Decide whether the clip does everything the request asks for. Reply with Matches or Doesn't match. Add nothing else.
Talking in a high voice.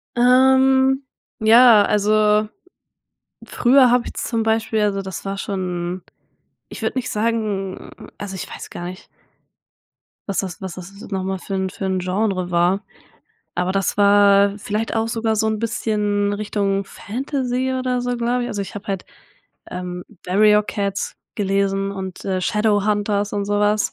Matches